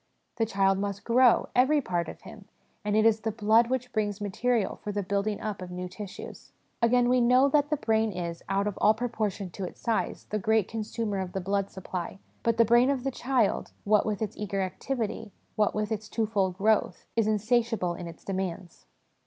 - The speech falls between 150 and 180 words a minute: No, average, 200 wpm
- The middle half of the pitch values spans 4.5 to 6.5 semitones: No, average, 3.0 semitones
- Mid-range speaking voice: No, high, 215 Hz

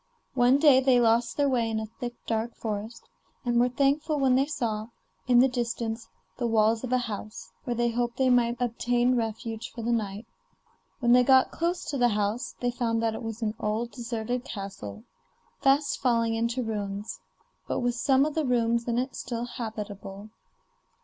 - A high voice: Yes, high, 235 Hz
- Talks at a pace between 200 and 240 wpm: No, average, 185 wpm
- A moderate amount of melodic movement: No, narrow, 2.0 semitones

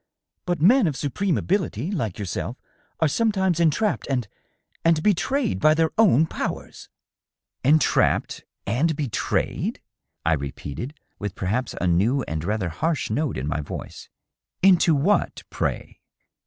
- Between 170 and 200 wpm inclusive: No, average, 145 wpm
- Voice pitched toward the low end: No, medium, 150 Hz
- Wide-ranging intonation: Yes, wide, 8.8 semitones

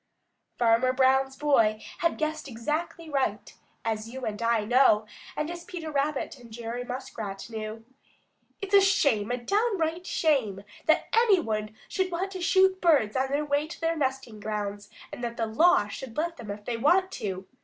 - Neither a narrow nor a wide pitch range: No, wide, 6.8 semitones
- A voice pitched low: No, very high, 265 Hz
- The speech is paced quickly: No, average, 180 wpm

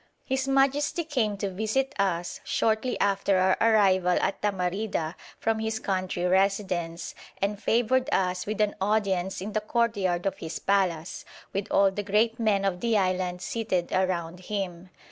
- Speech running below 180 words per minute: Yes, average, 155 wpm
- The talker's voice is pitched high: Yes, high, 195 Hz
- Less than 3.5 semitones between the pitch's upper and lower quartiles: Yes, average, 3.0 semitones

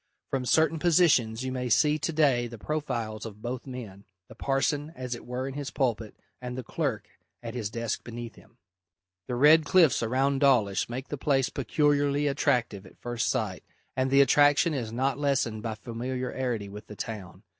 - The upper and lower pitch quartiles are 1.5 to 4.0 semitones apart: Yes, average, 3.5 semitones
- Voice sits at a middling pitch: No, low, 130 Hz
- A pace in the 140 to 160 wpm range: No, average, 180 wpm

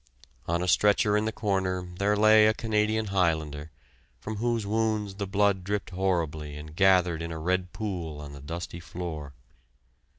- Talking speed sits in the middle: Yes, average, 165 wpm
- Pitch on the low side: Yes, very low, 95 Hz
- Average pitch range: Yes, average, 4.0 semitones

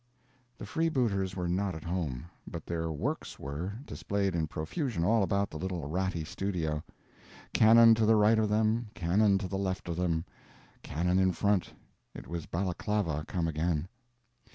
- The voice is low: Yes, very low, 95 Hz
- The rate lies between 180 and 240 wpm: No, average, 155 wpm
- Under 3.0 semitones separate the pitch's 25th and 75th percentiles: No, average, 3.8 semitones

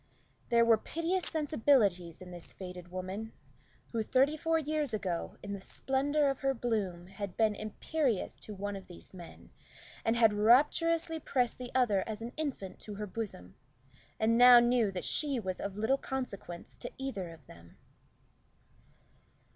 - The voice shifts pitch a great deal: Yes, wide, 5.8 semitones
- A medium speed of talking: Yes, average, 160 wpm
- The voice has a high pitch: Yes, high, 225 Hz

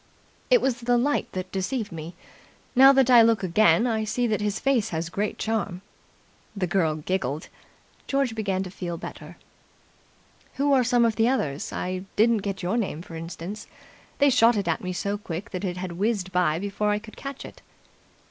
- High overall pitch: Yes, high, 205 Hz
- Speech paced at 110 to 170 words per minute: No, average, 190 wpm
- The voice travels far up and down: No, average, 4.5 semitones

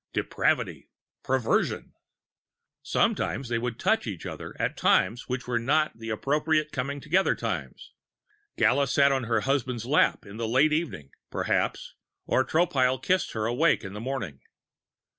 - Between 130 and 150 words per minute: Yes, average, 145 wpm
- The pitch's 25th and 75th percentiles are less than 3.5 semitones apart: No, average, 4.2 semitones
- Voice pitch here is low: Yes, low, 130 Hz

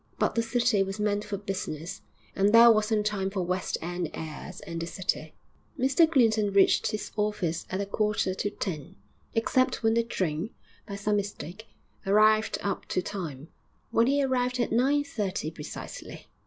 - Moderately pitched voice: No, high, 205 Hz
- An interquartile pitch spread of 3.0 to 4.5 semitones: Yes, average, 3.4 semitones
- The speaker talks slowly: No, average, 170 wpm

